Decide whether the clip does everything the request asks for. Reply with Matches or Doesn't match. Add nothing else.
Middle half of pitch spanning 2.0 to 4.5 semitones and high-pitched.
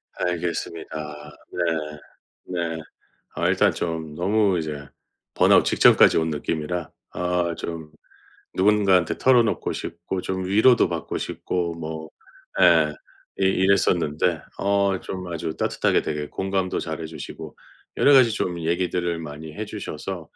Doesn't match